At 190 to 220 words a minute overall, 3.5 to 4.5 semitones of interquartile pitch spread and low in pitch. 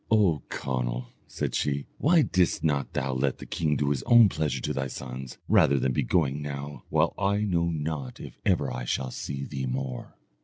Yes: average, 195 wpm; average, 3.8 semitones; very low, 70 Hz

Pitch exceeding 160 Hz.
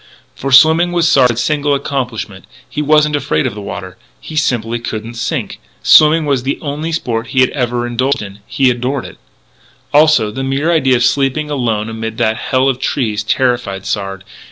No: low, 130 Hz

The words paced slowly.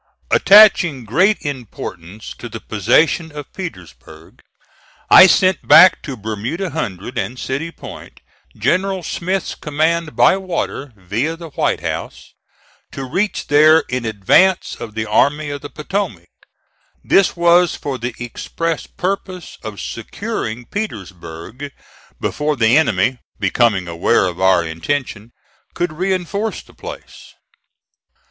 Yes: slow, 125 wpm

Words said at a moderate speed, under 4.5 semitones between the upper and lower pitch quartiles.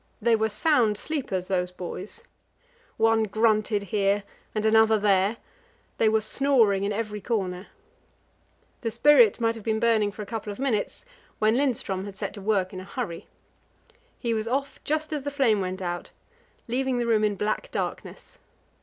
Yes: average, 170 wpm; average, 2.7 semitones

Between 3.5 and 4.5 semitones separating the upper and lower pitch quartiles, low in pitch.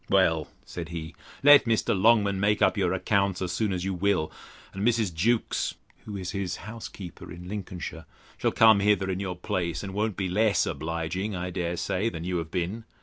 No: average, 3.0 semitones; very low, 95 Hz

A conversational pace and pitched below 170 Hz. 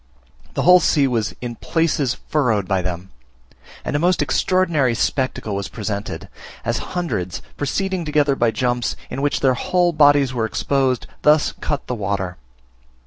Yes: average, 150 wpm; low, 135 Hz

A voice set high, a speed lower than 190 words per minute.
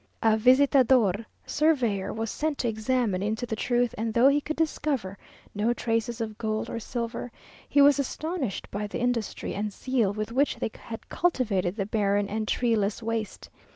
Yes: high, 230 Hz; average, 170 wpm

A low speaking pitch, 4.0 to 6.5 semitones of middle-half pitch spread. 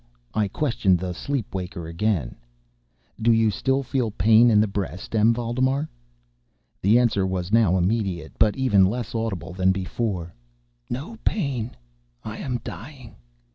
Yes: low, 110 Hz; average, 4.5 semitones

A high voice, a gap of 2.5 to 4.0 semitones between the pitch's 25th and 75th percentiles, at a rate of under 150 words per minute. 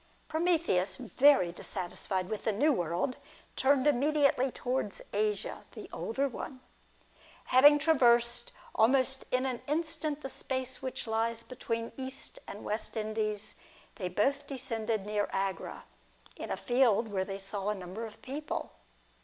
No: high, 235 Hz; average, 4.4 semitones; average, 140 wpm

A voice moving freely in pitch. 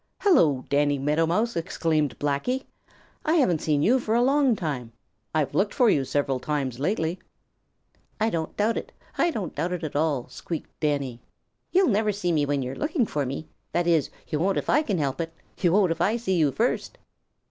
Yes: wide, 6.8 semitones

